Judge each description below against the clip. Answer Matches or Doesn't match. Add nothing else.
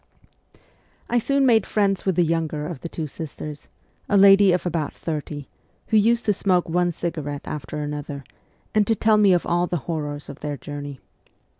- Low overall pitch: Doesn't match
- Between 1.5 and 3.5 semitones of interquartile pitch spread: Doesn't match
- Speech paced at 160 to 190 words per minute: Matches